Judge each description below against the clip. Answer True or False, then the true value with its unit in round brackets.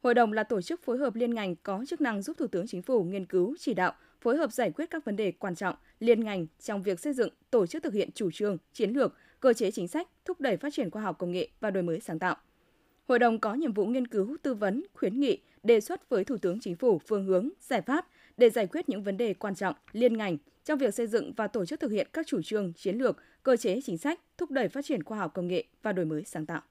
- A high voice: True (230 Hz)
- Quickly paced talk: True (280 wpm)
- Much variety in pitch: True (6.5 semitones)